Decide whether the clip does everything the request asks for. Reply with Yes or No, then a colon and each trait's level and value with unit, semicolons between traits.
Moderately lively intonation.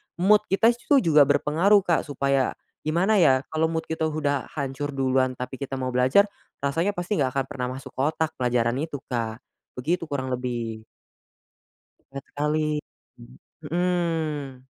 Yes: average, 4.0 semitones